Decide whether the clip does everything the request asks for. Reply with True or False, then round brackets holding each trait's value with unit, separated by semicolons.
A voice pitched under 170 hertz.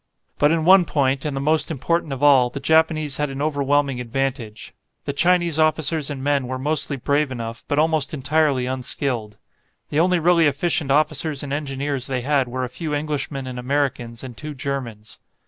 True (140 Hz)